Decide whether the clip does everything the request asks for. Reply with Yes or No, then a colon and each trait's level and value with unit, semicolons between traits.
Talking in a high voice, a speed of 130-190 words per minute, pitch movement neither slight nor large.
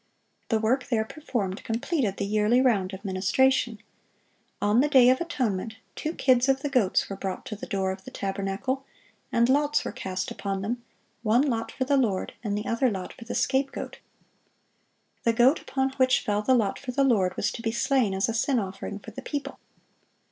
No: high, 230 Hz; average, 200 wpm; average, 4.8 semitones